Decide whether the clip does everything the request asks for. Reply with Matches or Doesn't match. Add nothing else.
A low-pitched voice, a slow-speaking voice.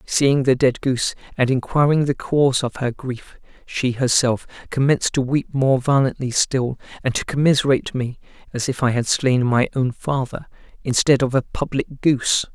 Doesn't match